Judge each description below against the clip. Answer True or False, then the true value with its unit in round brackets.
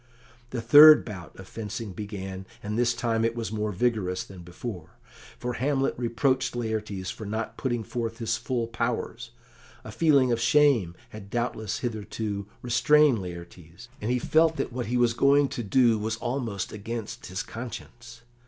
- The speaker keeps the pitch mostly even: False (3.0 semitones)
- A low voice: True (115 Hz)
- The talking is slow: False (160 wpm)